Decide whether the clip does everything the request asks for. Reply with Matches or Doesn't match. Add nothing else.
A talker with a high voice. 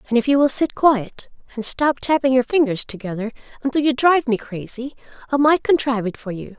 Matches